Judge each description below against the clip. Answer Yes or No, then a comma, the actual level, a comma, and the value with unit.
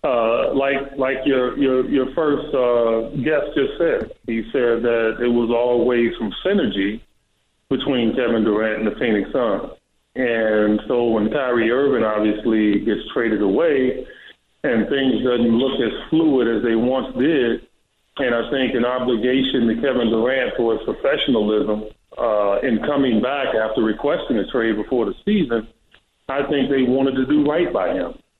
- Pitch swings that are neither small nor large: Yes, average, 3.2 semitones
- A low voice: Yes, low, 120 Hz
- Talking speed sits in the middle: Yes, average, 160 wpm